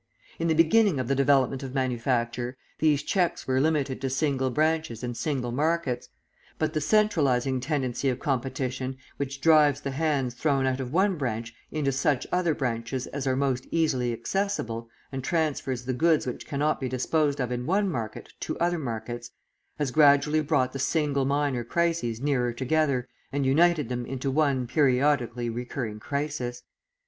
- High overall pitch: No, low, 135 Hz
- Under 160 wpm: No, average, 165 wpm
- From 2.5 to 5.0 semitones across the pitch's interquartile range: Yes, average, 3.5 semitones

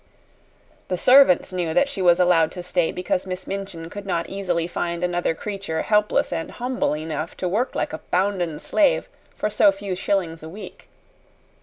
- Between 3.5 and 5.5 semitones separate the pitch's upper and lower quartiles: No, average, 2.9 semitones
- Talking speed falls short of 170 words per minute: No, average, 175 wpm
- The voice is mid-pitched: Yes, medium, 180 Hz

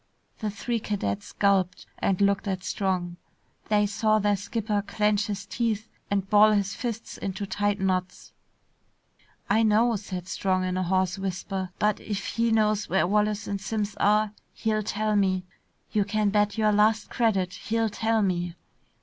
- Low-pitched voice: No, high, 205 Hz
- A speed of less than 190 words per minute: Yes, average, 160 wpm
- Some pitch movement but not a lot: No, narrow, 1.9 semitones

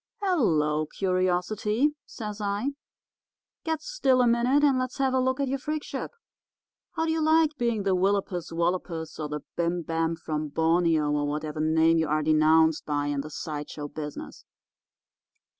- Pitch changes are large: Yes, wide, 8.7 semitones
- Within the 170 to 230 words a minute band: No, average, 160 wpm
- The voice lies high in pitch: No, medium, 175 Hz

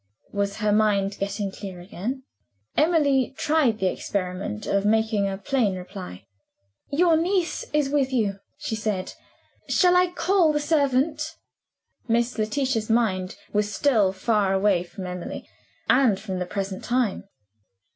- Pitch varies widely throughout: Yes, wide, 6.0 semitones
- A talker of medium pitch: No, high, 215 Hz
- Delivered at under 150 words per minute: Yes, slow, 135 wpm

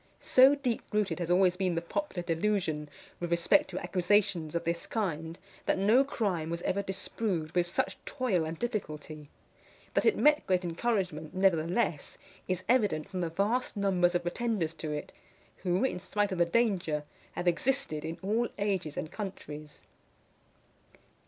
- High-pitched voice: No, medium, 180 Hz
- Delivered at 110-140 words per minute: No, average, 160 wpm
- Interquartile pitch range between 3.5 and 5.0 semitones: Yes, average, 4.0 semitones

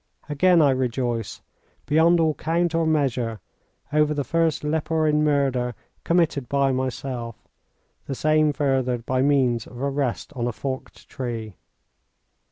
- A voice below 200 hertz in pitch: Yes, medium, 140 Hz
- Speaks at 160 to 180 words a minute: No, slow, 135 wpm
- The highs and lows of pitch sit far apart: No, average, 3.6 semitones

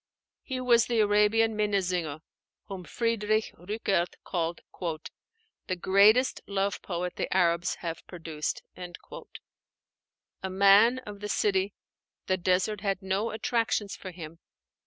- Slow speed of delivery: Yes, slow, 115 wpm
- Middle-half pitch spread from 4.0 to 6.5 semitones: No, average, 3.1 semitones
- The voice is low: No, high, 195 Hz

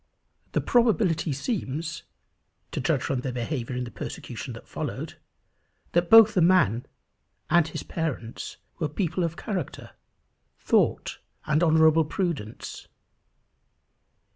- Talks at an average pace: No, slow, 115 wpm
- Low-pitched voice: No, medium, 160 Hz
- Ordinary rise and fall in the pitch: Yes, average, 5.0 semitones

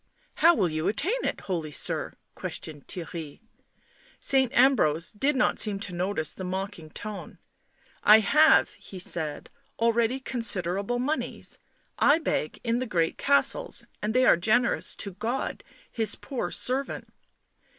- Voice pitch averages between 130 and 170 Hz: No, high, 215 Hz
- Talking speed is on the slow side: No, average, 145 wpm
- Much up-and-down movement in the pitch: Yes, wide, 6.4 semitones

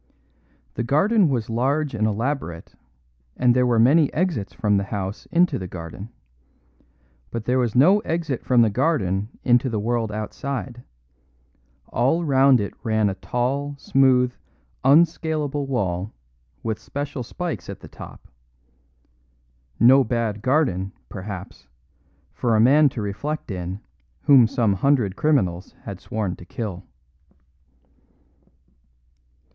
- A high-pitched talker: No, low, 120 Hz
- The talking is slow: Yes, slow, 125 wpm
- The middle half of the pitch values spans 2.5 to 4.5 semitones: No, average, 5.3 semitones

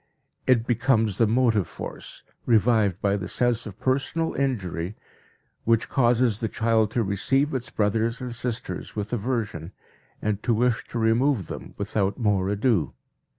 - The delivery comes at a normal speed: Yes, average, 150 wpm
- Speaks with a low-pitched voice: Yes, low, 115 Hz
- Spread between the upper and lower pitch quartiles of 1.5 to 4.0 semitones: Yes, average, 3.2 semitones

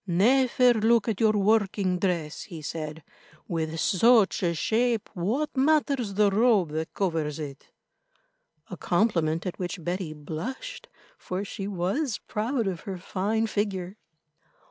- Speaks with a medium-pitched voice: No, high, 195 Hz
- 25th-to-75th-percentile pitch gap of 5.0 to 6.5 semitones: Yes, average, 5.3 semitones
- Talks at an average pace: No, slow, 130 wpm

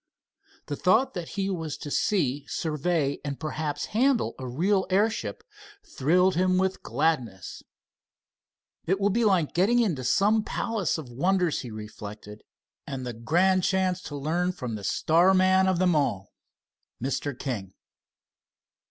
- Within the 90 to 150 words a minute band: Yes, average, 145 wpm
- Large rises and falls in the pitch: Yes, wide, 5.9 semitones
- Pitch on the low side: No, medium, 165 Hz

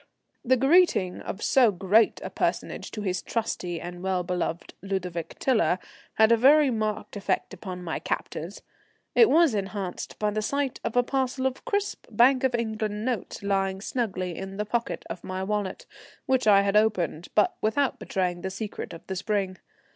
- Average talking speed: Yes, average, 175 wpm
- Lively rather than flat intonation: No, average, 4.4 semitones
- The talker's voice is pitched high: Yes, high, 210 Hz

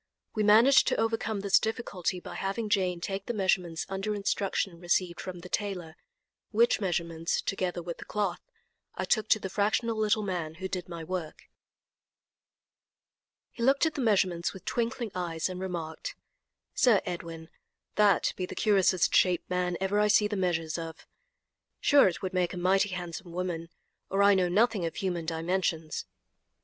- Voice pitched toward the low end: No, medium, 185 Hz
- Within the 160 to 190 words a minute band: Yes, average, 165 wpm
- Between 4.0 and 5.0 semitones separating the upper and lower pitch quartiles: No, average, 3.1 semitones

